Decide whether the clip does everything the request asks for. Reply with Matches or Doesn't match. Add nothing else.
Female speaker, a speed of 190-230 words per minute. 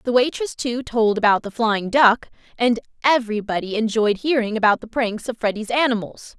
Doesn't match